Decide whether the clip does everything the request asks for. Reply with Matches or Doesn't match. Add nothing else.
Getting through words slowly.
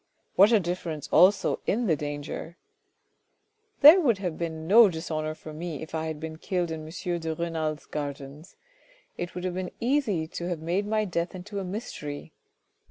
Doesn't match